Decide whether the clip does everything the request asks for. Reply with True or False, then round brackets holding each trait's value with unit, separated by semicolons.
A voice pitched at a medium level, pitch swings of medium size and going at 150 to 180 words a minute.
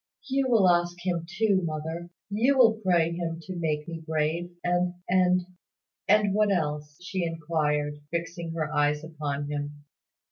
True (170 Hz; 3.2 semitones; 155 wpm)